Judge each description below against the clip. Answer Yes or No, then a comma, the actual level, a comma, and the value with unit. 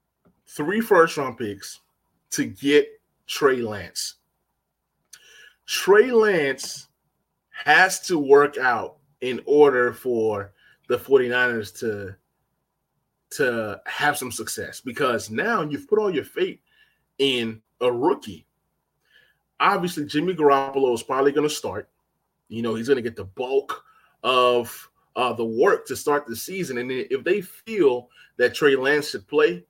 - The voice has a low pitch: No, medium, 150 Hz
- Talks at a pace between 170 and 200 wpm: No, slow, 135 wpm